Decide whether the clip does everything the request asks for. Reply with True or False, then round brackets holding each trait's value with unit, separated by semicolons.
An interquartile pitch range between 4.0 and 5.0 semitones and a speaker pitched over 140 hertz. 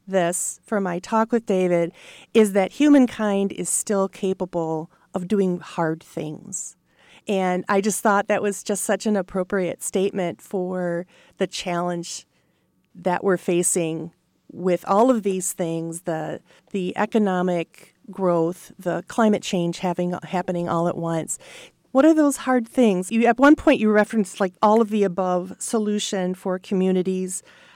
False (2.8 semitones; 190 Hz)